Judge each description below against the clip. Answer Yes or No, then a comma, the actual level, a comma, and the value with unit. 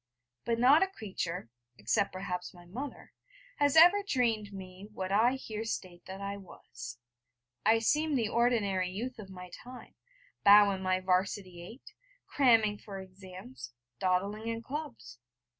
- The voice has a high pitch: Yes, high, 200 Hz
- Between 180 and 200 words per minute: No, average, 145 wpm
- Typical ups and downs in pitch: Yes, average, 4.2 semitones